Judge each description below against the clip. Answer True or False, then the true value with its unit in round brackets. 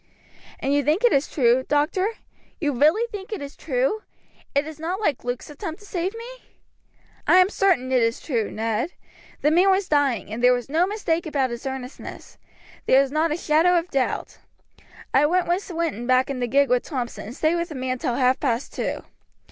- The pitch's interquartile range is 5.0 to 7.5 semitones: True (5.3 semitones)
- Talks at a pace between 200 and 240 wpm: True (205 wpm)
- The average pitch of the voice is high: True (290 Hz)